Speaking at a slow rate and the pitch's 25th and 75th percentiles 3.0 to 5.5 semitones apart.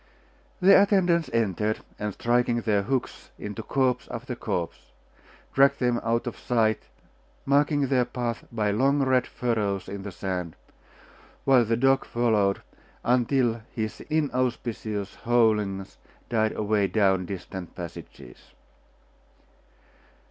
Yes: slow, 115 wpm; average, 3.8 semitones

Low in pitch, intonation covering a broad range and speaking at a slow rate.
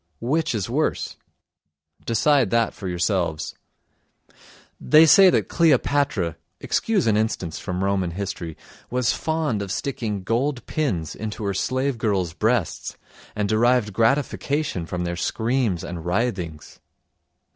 Yes: low, 110 Hz; wide, 6.3 semitones; slow, 125 wpm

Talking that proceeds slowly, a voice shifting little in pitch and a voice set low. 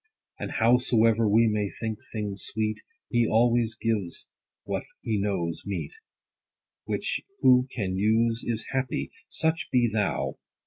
Yes: slow, 130 wpm; narrow, 2.3 semitones; low, 110 Hz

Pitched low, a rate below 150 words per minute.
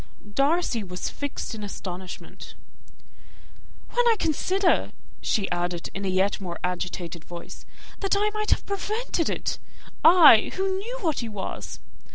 No: high, 235 Hz; average, 140 wpm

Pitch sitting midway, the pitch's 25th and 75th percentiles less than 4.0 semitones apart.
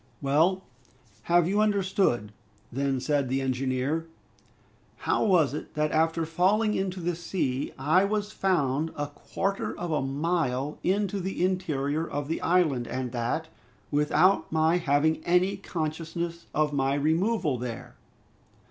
No: medium, 160 Hz; average, 4.6 semitones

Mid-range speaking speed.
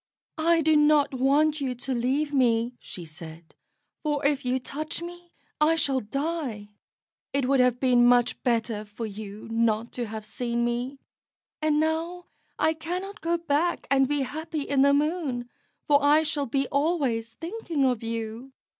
Yes: average, 165 wpm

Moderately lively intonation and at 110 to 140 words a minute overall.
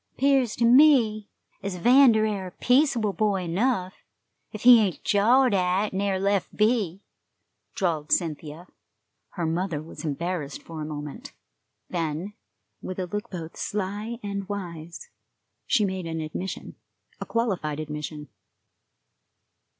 Yes: average, 4.6 semitones; slow, 135 wpm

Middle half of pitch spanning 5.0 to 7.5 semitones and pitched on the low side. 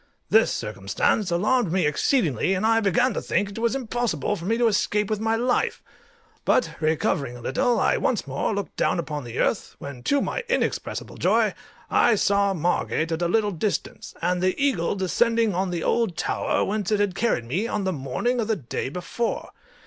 No: average, 5.3 semitones; high, 200 Hz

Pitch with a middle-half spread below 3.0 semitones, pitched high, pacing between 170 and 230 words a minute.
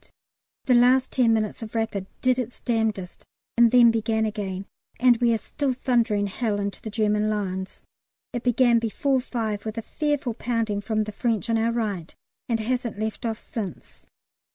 Yes: narrow, 2.5 semitones; high, 225 Hz; average, 175 wpm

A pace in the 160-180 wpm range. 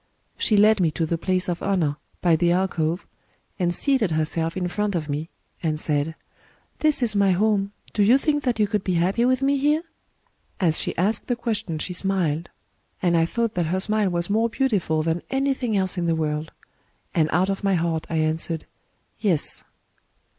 No: average, 195 wpm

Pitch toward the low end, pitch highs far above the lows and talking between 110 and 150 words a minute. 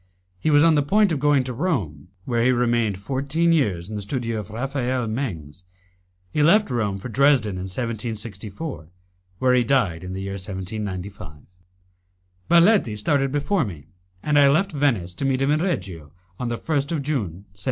No: low, 120 Hz; wide, 6.6 semitones; average, 180 wpm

